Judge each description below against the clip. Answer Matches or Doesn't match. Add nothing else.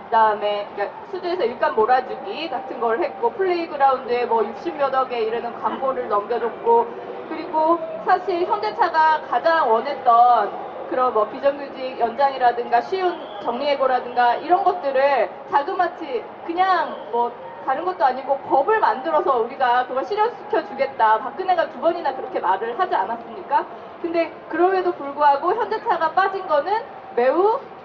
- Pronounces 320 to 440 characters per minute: Matches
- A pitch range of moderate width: Doesn't match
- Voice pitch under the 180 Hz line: Doesn't match